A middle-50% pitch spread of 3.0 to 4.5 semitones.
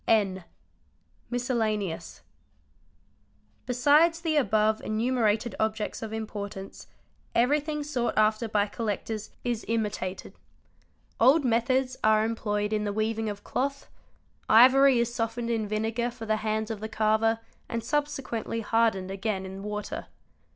No: narrow, 2.4 semitones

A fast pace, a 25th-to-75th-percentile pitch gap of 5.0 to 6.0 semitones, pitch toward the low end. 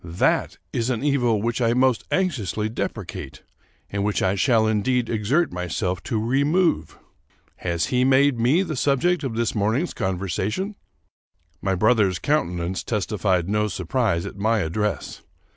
No: average, 145 wpm; average, 5.3 semitones; low, 110 Hz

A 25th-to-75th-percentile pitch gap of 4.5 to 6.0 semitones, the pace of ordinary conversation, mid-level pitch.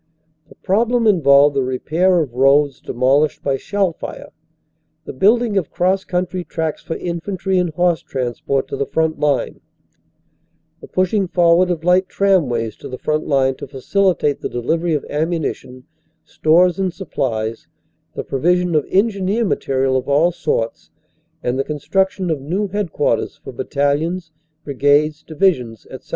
Yes: average, 4.9 semitones; average, 150 wpm; medium, 160 Hz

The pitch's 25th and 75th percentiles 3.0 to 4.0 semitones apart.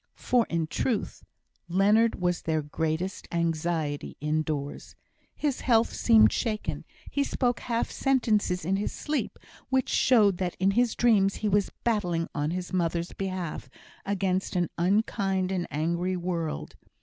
No: average, 4.4 semitones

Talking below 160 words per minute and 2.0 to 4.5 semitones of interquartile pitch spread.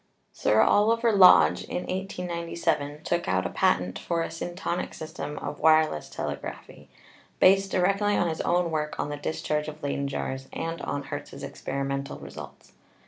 Yes: average, 150 wpm; average, 4.0 semitones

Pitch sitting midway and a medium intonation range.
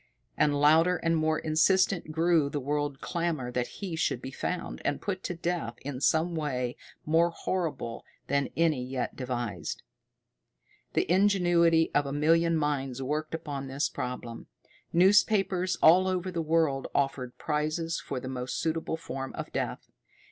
Yes: medium, 155 Hz; average, 3.8 semitones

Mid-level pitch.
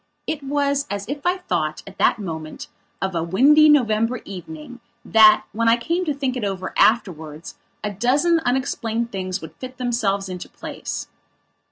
No: high, 230 Hz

